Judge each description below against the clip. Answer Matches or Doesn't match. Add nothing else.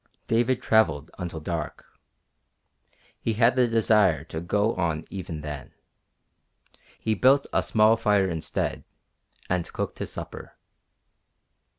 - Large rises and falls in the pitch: Matches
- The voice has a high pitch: Doesn't match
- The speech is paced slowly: Matches